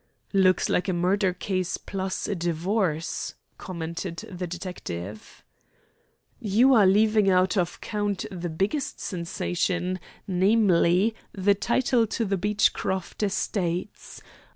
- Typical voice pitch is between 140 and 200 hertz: Yes, high, 190 Hz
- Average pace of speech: No, slow, 110 wpm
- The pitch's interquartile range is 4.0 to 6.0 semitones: No, narrow, 2.6 semitones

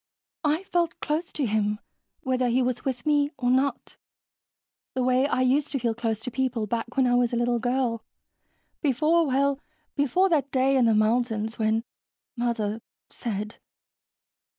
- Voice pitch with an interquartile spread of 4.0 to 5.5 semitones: No, average, 3.2 semitones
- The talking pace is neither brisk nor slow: Yes, average, 160 wpm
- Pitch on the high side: Yes, very high, 250 Hz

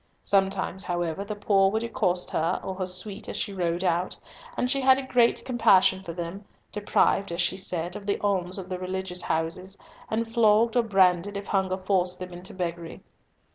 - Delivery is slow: No, average, 190 wpm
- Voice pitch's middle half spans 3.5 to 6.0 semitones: No, narrow, 2.4 semitones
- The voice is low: No, high, 190 Hz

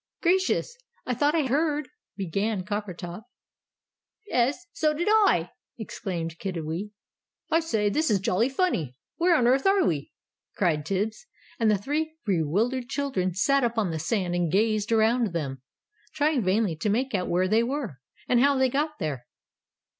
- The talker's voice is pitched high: Yes, high, 220 Hz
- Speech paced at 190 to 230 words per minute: No, average, 160 wpm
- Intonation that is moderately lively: No, wide, 7.5 semitones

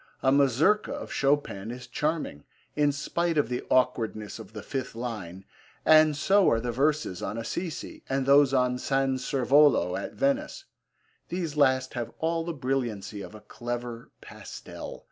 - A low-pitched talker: Yes, low, 130 Hz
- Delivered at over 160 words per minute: No, average, 155 wpm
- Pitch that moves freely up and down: No, average, 4.3 semitones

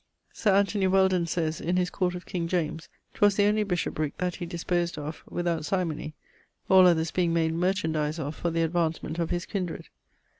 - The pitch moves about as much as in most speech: No, narrow, 2.3 semitones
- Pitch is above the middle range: No, medium, 175 Hz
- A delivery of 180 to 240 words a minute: Yes, average, 185 wpm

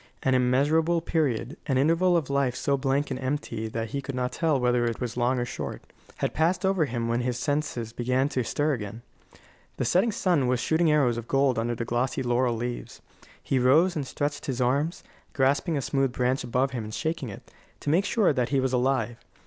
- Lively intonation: No, average, 3.4 semitones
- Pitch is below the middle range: Yes, low, 130 Hz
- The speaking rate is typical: No, fast, 210 wpm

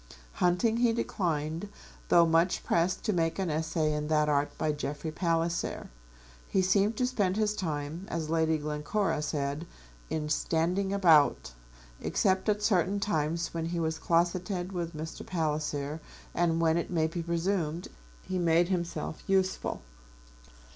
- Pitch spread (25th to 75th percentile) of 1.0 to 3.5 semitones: Yes, average, 3.2 semitones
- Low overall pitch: No, medium, 170 Hz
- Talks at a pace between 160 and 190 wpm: No, average, 145 wpm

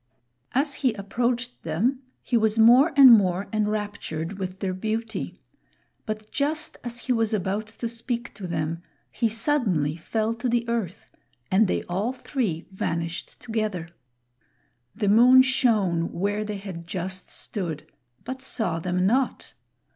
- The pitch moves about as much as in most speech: Yes, average, 4.4 semitones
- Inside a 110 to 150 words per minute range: Yes, average, 140 wpm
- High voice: Yes, high, 215 Hz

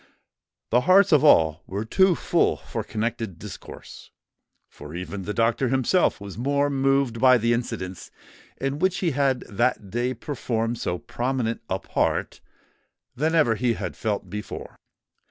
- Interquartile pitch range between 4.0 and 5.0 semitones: Yes, average, 4.5 semitones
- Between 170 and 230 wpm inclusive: No, average, 150 wpm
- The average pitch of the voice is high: No, low, 120 Hz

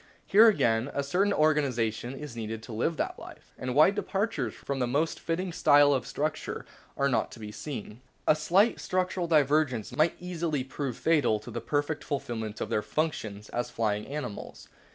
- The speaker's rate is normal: Yes, average, 175 wpm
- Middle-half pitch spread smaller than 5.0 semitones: No, wide, 5.5 semitones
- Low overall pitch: No, medium, 145 Hz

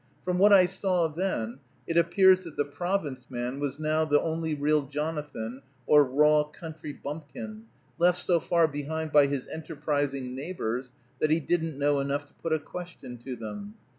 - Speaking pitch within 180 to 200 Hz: No, medium, 150 Hz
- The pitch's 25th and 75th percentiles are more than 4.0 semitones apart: No, average, 3.2 semitones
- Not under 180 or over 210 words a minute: No, average, 170 wpm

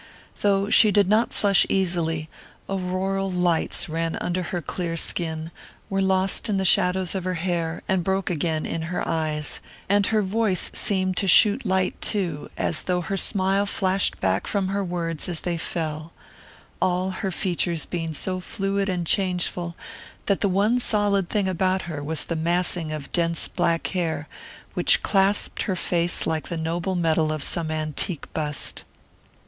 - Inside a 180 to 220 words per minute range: No, average, 165 wpm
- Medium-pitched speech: Yes, medium, 180 Hz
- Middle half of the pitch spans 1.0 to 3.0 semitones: Yes, average, 2.7 semitones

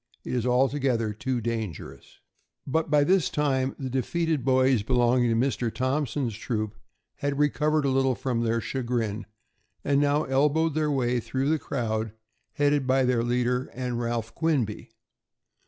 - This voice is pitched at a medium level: No, low, 130 Hz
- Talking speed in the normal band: Yes, average, 150 wpm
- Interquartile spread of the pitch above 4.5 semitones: No, average, 3.3 semitones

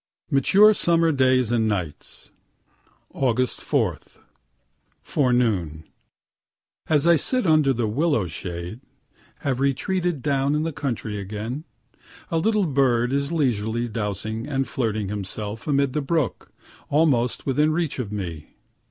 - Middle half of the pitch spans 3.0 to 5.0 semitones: No, wide, 5.6 semitones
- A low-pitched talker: Yes, low, 130 Hz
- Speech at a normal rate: No, slow, 125 wpm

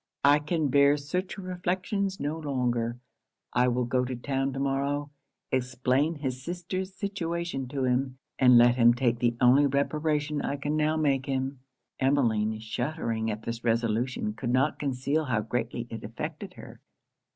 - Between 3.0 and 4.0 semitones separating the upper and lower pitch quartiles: Yes, average, 3.7 semitones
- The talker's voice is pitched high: No, low, 135 Hz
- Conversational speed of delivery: Yes, average, 155 wpm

